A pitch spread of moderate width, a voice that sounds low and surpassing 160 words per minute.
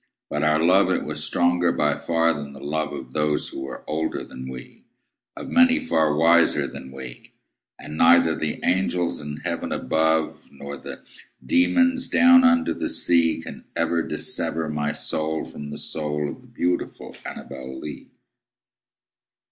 No: average, 3.0 semitones; very low, 80 Hz; average, 155 wpm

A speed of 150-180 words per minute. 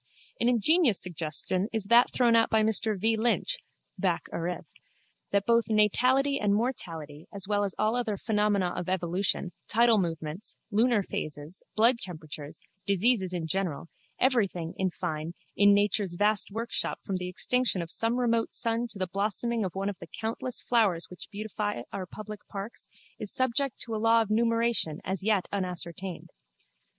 Yes: average, 160 wpm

